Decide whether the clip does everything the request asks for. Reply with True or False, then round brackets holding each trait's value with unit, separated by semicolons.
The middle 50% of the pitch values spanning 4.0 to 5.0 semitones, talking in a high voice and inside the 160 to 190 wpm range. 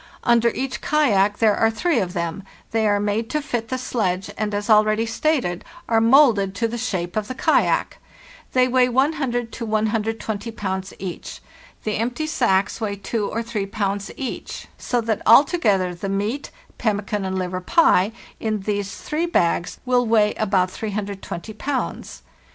False (3.5 semitones; 215 Hz; 165 wpm)